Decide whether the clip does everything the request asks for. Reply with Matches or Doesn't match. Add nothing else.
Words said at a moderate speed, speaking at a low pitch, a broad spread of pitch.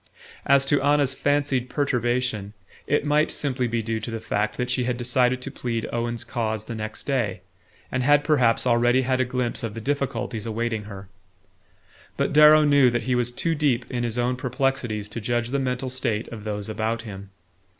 Doesn't match